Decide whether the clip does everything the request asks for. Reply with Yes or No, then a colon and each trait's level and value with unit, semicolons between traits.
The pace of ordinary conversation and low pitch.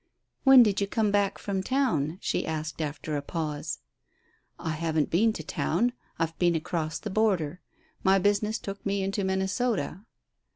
No: average, 160 wpm; high, 190 Hz